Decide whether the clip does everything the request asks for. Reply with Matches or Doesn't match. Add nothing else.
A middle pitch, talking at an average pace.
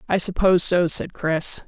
Matches